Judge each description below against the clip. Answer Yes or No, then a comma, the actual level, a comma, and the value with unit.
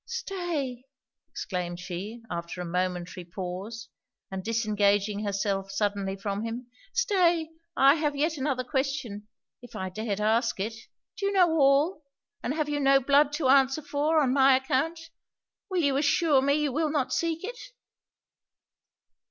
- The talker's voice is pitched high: Yes, very high, 265 Hz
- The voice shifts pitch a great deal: Yes, wide, 7.0 semitones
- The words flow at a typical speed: Yes, average, 150 wpm